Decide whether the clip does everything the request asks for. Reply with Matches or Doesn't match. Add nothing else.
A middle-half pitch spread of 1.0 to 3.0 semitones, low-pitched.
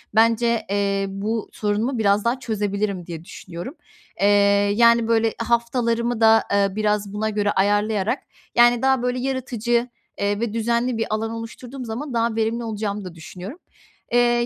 Doesn't match